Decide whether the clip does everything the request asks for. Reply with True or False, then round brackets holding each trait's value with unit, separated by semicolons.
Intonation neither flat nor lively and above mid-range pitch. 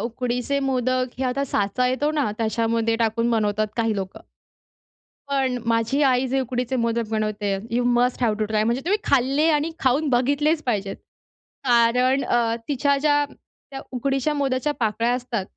True (3.0 semitones; 250 Hz)